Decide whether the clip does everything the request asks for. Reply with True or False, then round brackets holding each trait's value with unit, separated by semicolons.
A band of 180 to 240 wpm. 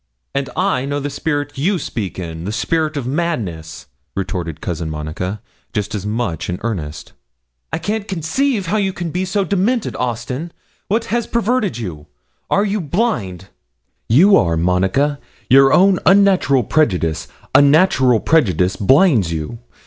False (145 wpm)